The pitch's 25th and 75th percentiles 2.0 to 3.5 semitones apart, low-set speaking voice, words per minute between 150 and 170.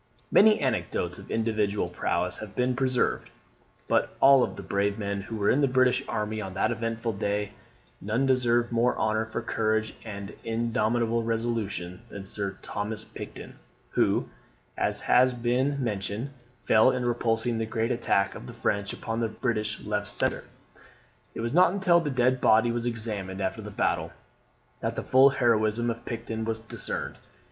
Yes: narrow, 2.5 semitones; low, 115 Hz; average, 165 wpm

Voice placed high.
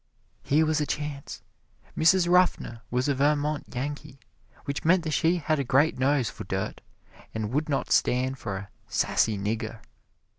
No: medium, 140 Hz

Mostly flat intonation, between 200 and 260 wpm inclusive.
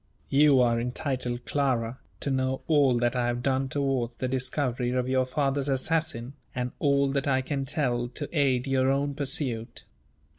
No: narrow, 2.1 semitones; average, 170 wpm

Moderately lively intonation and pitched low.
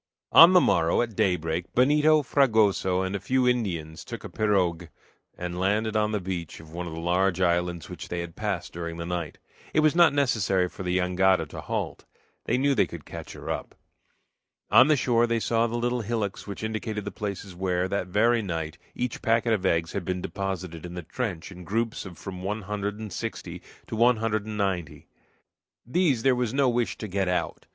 Yes: average, 4.6 semitones; low, 100 Hz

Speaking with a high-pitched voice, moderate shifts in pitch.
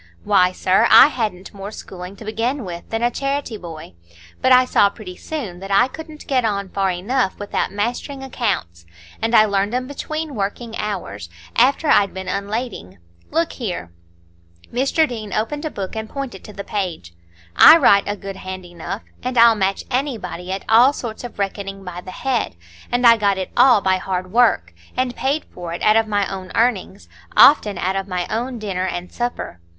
Yes: high, 210 Hz; average, 4.6 semitones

